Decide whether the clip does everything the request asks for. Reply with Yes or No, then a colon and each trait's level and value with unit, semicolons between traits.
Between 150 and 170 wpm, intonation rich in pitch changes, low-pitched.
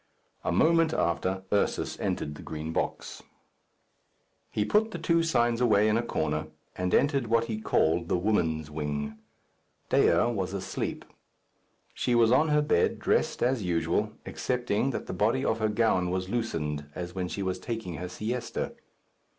Yes: average, 160 wpm; wide, 5.8 semitones; low, 105 Hz